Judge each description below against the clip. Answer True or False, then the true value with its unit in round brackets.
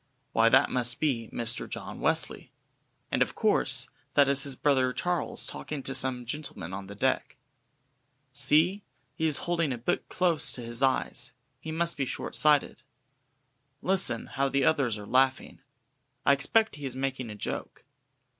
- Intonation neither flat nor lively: True (3.7 semitones)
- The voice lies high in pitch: False (135 Hz)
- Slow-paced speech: False (165 wpm)